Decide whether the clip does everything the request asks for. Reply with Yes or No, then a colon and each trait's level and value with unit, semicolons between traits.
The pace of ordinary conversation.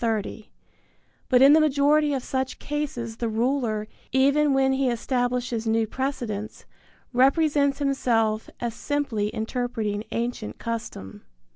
No: slow, 120 wpm